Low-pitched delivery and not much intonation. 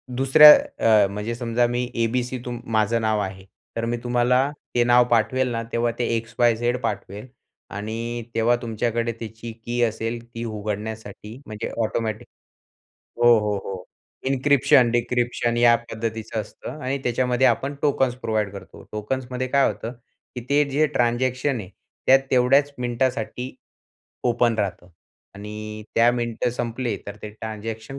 Yes: low, 120 Hz; narrow, 2.1 semitones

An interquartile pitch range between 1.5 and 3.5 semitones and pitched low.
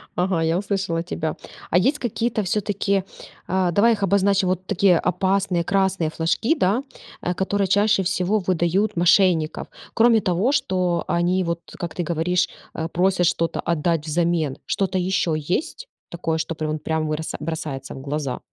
No: average, 3.0 semitones; medium, 180 Hz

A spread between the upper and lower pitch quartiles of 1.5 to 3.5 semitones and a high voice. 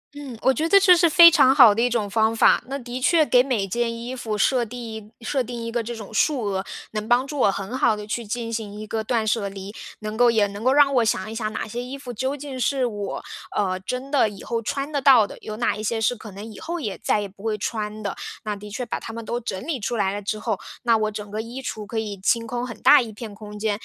Yes: average, 3.1 semitones; high, 230 Hz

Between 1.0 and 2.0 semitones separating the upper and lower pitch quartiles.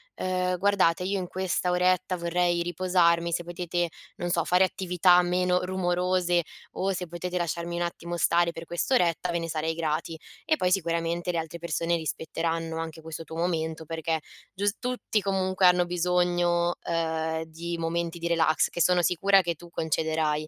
Yes: narrow, 1.6 semitones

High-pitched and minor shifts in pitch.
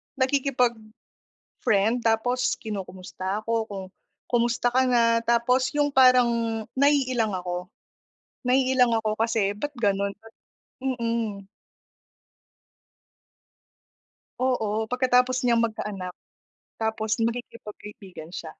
No: high, 230 Hz; average, 3.1 semitones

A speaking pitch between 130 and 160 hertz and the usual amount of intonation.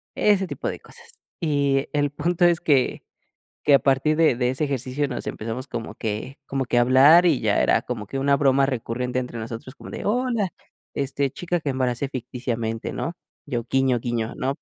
Yes: low, 135 Hz; average, 3.1 semitones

